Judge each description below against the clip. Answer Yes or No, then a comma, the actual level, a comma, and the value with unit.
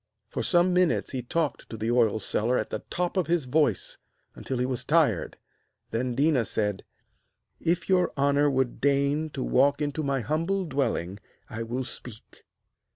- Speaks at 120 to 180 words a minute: Yes, average, 165 wpm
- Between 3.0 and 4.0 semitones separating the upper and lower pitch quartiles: No, average, 4.8 semitones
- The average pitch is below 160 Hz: Yes, medium, 140 Hz